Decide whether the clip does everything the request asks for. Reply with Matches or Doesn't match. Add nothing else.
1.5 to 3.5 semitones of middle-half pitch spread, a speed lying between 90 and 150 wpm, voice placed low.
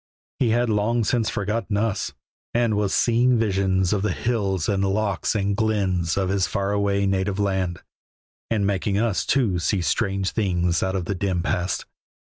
Doesn't match